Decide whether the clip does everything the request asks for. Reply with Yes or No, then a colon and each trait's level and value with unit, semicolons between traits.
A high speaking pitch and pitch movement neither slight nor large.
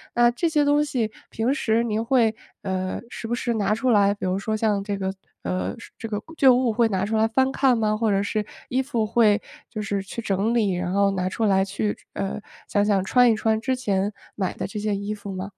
Yes: high, 215 Hz; average, 3.0 semitones